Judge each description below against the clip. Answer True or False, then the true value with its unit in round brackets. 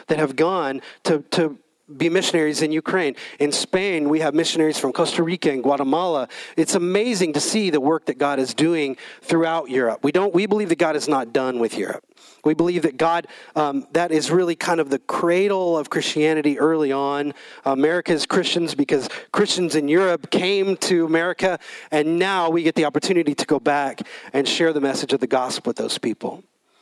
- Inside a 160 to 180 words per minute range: False (190 wpm)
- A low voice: False (160 Hz)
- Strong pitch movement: False (2.9 semitones)